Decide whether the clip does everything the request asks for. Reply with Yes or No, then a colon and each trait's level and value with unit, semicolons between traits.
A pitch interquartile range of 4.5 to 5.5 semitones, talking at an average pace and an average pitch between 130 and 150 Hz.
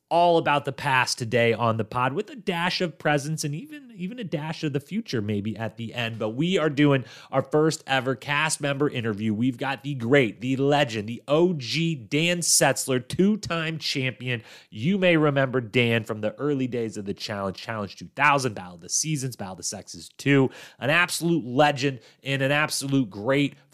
Yes: average, 4.9 semitones; average, 195 wpm; low, 135 Hz